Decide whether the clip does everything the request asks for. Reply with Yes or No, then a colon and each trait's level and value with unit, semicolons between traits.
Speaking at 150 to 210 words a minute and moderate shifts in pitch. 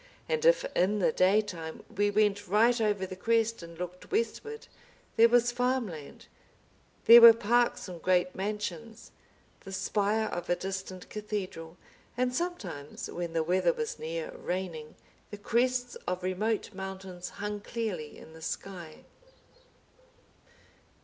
No: slow, 135 wpm; average, 4.3 semitones